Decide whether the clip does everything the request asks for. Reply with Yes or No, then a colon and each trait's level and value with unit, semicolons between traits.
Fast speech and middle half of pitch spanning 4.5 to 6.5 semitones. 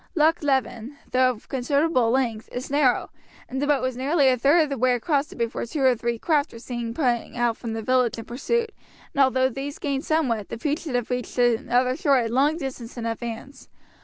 No: fast, 215 wpm; average, 3.1 semitones